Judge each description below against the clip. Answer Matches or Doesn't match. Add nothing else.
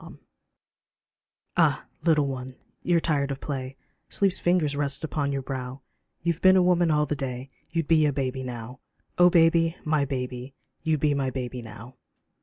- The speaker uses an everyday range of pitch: Matches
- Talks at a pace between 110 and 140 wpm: Doesn't match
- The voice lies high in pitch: Doesn't match